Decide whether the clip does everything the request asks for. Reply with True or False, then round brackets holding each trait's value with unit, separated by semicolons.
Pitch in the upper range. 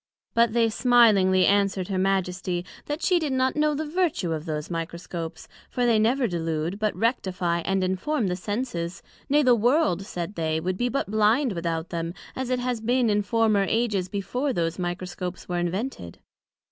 True (200 Hz)